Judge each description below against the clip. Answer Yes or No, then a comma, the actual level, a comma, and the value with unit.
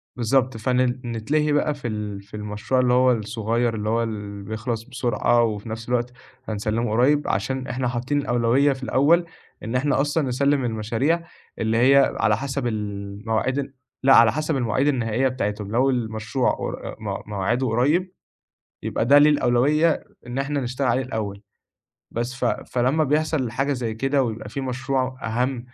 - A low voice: Yes, low, 125 Hz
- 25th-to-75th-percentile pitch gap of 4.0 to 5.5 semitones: No, average, 3.4 semitones